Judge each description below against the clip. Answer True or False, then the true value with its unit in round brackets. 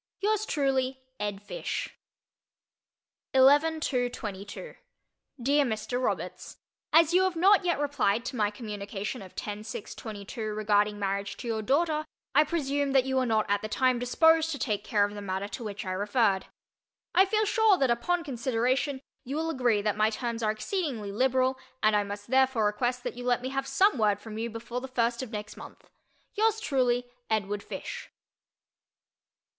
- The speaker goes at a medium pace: True (180 wpm)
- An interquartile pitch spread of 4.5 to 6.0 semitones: True (5.1 semitones)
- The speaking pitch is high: True (245 Hz)